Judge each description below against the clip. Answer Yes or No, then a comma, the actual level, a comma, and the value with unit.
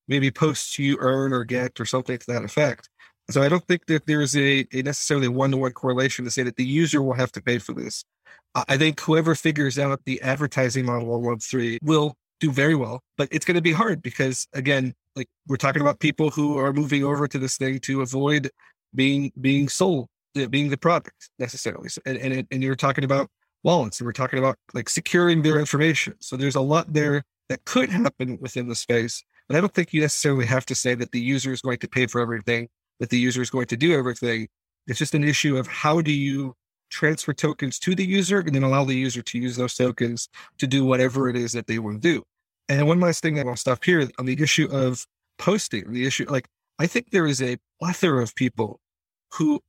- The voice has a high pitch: No, low, 135 Hz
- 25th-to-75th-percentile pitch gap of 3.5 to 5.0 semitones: No, average, 3.1 semitones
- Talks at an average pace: No, fast, 230 wpm